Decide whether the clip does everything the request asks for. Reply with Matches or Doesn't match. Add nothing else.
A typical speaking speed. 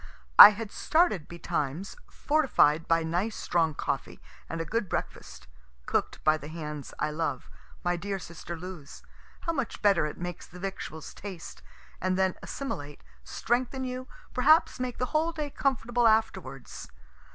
Matches